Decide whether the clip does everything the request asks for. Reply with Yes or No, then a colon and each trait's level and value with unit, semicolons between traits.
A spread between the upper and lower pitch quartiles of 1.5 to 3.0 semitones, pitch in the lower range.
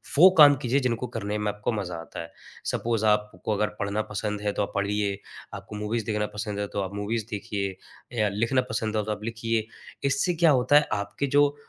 Yes: narrow, 2.4 semitones; low, 105 Hz